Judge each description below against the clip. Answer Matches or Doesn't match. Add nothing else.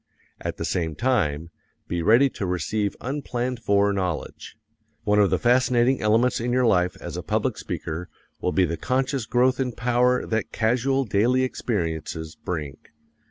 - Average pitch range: Doesn't match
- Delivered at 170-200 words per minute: Doesn't match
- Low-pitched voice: Matches